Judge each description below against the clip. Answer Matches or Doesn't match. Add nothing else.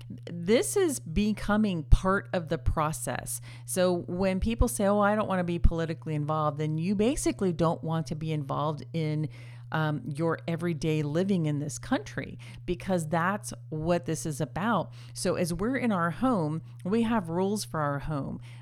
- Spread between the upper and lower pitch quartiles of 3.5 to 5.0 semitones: Matches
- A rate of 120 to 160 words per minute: Doesn't match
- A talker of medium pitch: Matches